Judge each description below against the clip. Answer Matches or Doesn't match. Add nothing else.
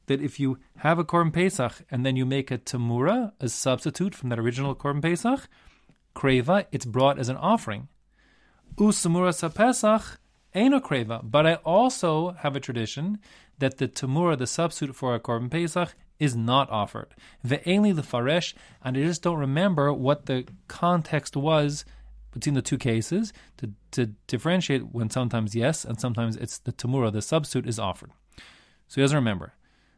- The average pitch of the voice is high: Doesn't match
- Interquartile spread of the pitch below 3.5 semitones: Doesn't match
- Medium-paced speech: Matches